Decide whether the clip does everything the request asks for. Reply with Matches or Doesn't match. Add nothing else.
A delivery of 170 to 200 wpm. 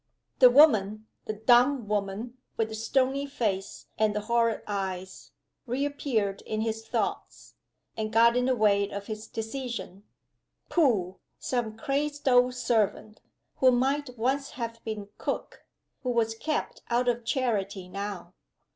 Doesn't match